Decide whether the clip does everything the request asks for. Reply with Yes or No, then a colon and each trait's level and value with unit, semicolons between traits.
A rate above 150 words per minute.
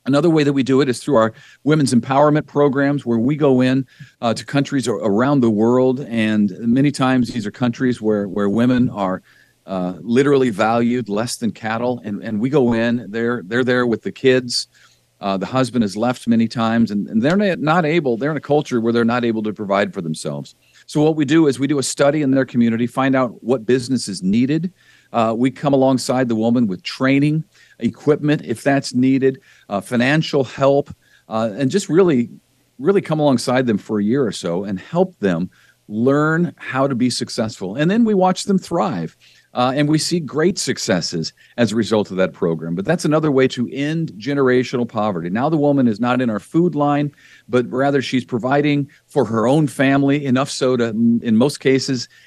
Yes: average, 200 wpm